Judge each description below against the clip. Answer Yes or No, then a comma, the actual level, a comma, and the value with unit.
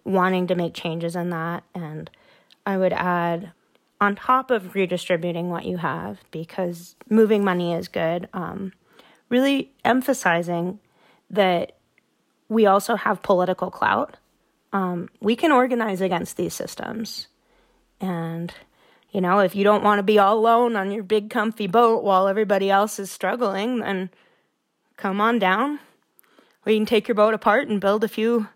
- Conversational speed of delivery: Yes, average, 155 wpm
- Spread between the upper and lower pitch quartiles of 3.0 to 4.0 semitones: Yes, average, 3.6 semitones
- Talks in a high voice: Yes, high, 200 Hz